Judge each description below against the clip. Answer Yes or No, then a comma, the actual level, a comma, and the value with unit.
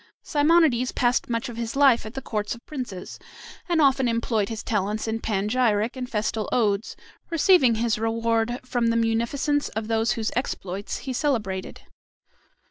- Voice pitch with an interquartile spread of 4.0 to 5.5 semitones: No, average, 2.8 semitones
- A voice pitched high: Yes, high, 230 Hz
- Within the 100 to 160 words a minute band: Yes, average, 155 wpm